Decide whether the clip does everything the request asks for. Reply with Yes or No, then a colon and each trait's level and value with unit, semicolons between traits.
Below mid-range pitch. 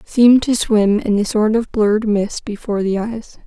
No: high, 215 Hz